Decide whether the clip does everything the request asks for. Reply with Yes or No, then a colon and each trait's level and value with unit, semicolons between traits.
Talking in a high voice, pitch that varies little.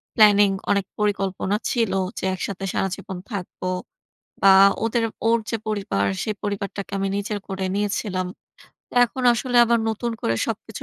Yes: high, 200 Hz; narrow, 2.1 semitones